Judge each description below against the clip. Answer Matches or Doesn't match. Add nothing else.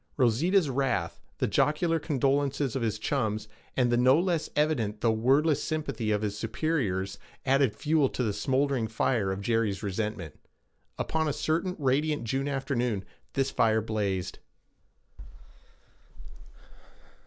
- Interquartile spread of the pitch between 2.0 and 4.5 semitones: Doesn't match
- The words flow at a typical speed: Doesn't match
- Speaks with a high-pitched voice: Doesn't match